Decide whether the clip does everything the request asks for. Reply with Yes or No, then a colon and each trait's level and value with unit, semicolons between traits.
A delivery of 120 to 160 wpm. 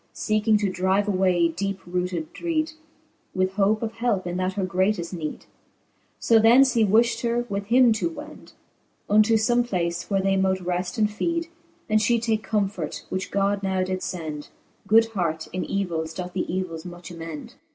No: average, 175 wpm